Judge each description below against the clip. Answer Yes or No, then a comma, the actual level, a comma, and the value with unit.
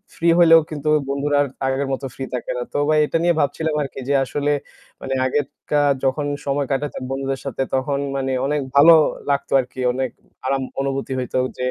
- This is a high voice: No, medium, 140 Hz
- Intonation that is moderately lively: No, narrow, 1.7 semitones